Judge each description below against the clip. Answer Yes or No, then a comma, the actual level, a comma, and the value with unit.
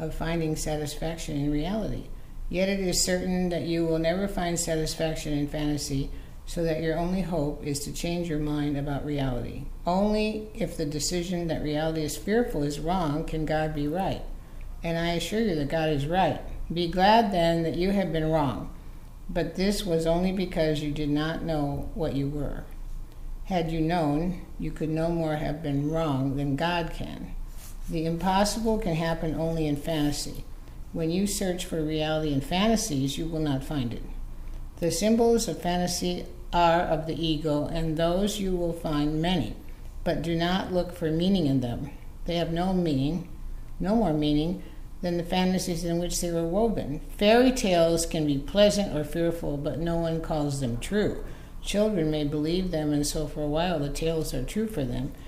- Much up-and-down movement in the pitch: No, average, 2.9 semitones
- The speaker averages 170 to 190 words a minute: Yes, average, 180 wpm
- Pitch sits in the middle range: Yes, medium, 160 Hz